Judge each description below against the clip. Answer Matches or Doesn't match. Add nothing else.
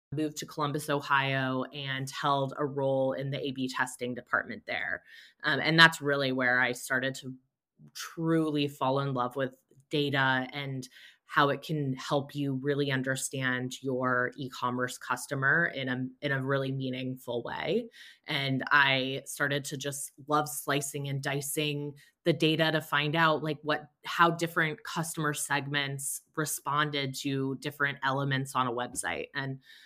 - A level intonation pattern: Matches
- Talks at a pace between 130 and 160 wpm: Matches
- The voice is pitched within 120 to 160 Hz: Matches